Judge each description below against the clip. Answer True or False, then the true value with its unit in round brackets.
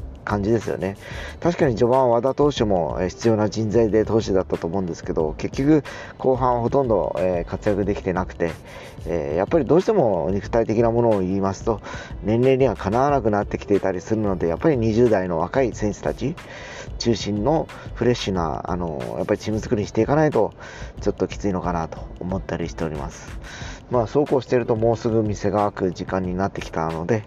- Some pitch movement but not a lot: True (3.8 semitones)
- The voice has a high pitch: False (110 Hz)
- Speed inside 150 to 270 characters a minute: False (380 characters per minute)